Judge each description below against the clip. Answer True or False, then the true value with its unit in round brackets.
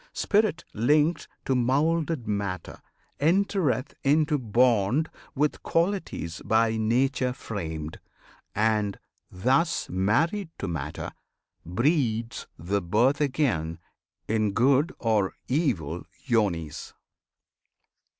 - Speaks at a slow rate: True (90 wpm)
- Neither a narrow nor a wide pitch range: False (6.7 semitones)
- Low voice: True (120 Hz)